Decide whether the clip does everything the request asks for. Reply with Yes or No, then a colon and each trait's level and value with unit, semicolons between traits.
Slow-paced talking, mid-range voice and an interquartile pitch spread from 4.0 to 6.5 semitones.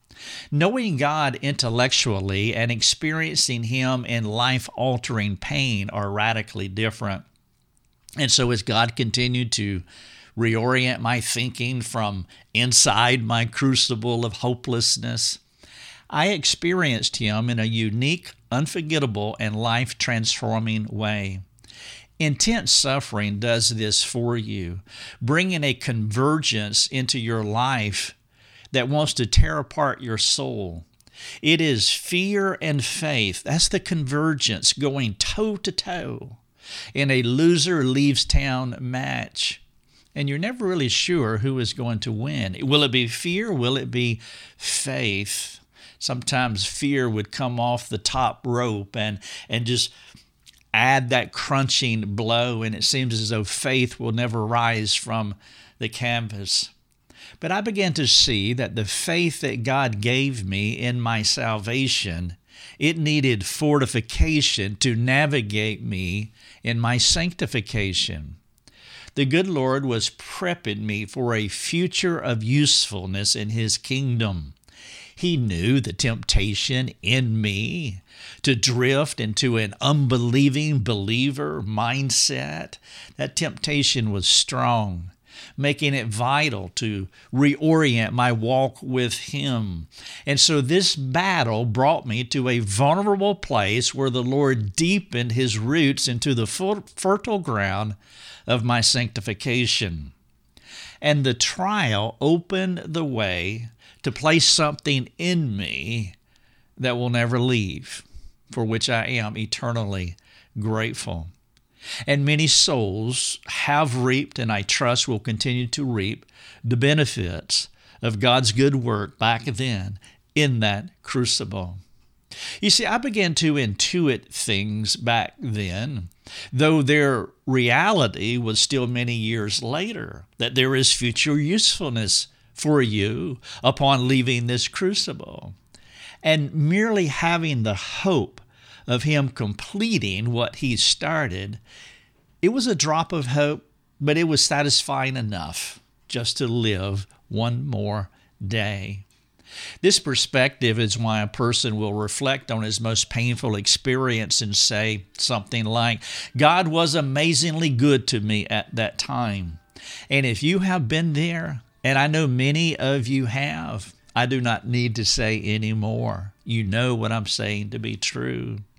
No: slow, 130 wpm; low, 120 Hz; average, 4.3 semitones